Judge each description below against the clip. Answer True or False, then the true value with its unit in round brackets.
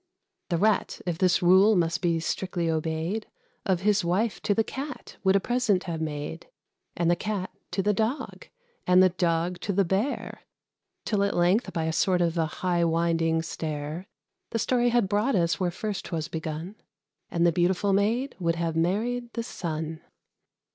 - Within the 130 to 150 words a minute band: False (175 wpm)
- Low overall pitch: False (180 Hz)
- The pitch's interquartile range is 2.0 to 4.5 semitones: True (3.8 semitones)